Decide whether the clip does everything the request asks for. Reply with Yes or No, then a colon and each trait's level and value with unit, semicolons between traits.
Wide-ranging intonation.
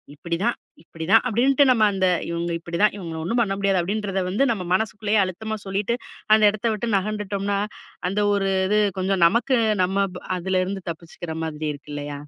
No: average, 3.8 semitones